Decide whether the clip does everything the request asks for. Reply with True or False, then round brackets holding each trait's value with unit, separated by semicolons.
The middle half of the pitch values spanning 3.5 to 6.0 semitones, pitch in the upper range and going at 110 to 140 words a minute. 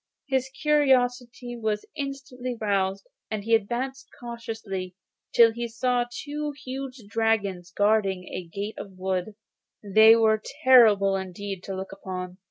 True (4.2 semitones; 225 Hz; 135 wpm)